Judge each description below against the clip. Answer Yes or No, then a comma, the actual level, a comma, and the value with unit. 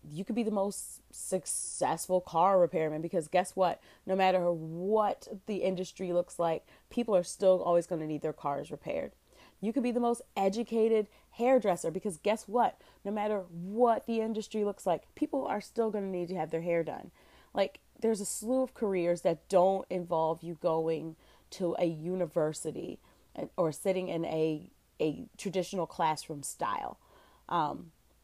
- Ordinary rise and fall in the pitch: Yes, average, 4.1 semitones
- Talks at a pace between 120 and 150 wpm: No, average, 170 wpm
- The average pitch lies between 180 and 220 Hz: Yes, medium, 185 Hz